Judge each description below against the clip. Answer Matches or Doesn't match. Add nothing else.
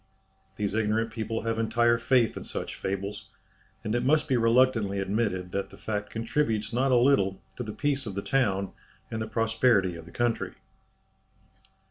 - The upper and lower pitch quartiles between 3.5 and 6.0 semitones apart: Doesn't match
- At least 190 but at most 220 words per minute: Doesn't match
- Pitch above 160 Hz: Doesn't match